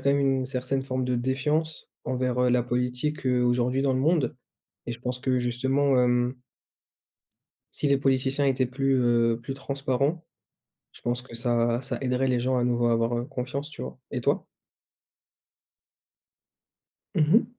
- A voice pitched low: Yes, low, 130 Hz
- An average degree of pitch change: No, narrow, 1.9 semitones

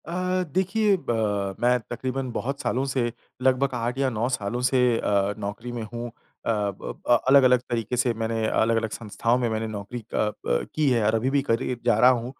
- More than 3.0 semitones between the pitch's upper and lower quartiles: No, average, 2.7 semitones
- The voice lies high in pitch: No, low, 120 Hz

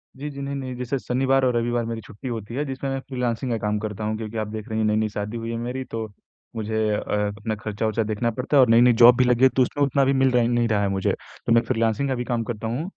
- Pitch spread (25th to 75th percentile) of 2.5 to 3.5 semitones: Yes, average, 2.9 semitones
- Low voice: Yes, low, 115 Hz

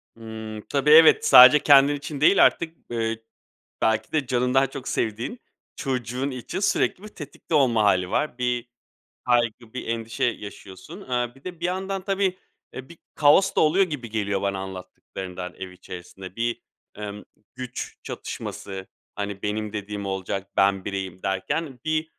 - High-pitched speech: No, low, 120 Hz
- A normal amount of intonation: No, wide, 6.3 semitones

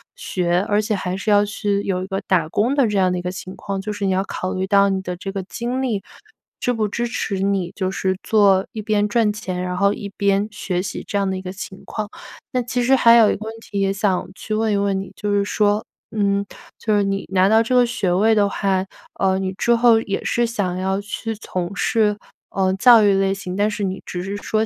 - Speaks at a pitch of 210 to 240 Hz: No, high, 200 Hz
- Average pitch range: No, narrow, 2.1 semitones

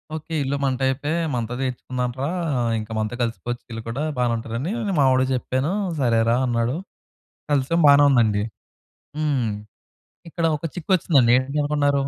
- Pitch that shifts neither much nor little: Yes, average, 3.3 semitones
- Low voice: Yes, low, 130 Hz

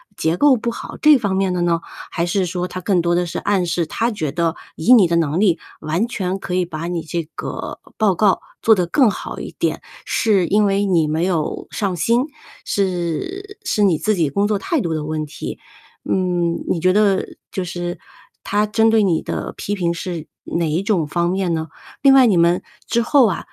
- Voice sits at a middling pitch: Yes, medium, 180 Hz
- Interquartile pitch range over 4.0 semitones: No, average, 3.7 semitones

